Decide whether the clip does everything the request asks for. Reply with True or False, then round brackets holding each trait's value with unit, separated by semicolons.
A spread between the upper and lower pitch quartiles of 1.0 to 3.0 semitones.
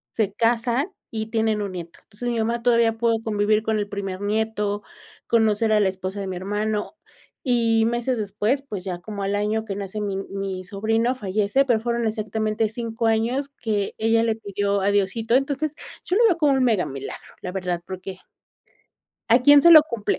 True (2.6 semitones)